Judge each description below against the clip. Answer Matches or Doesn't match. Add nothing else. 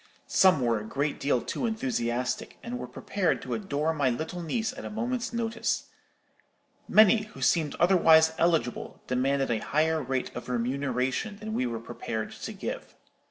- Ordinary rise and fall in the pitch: Doesn't match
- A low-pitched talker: Doesn't match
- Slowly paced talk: Doesn't match